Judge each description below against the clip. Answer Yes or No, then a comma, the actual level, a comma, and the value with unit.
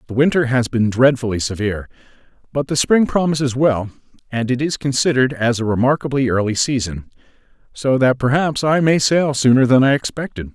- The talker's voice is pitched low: Yes, low, 130 Hz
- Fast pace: No, average, 170 wpm